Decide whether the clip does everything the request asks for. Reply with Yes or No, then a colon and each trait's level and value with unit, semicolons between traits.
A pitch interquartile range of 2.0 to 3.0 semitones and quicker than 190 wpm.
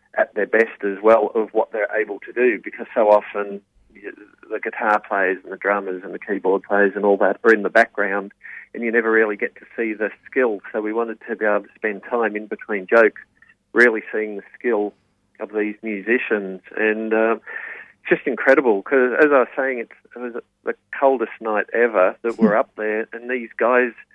Yes: narrow, 2.5 semitones; fast, 205 wpm